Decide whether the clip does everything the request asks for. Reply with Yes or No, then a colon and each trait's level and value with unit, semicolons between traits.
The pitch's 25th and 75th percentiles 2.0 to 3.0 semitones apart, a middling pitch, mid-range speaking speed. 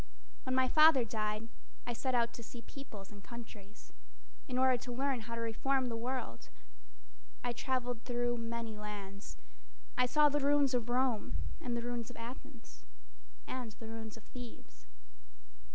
No: narrow, 2.4 semitones; high, 240 Hz; average, 160 wpm